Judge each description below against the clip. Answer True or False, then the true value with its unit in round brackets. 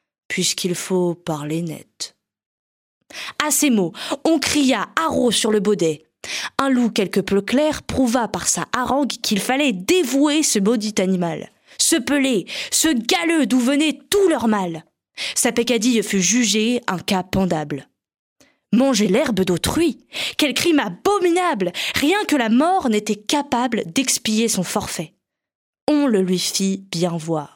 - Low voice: False (235 Hz)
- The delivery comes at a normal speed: False (140 wpm)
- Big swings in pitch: True (7.1 semitones)